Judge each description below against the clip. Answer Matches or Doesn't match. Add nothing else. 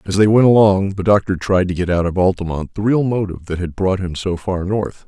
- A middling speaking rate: Doesn't match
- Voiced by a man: Matches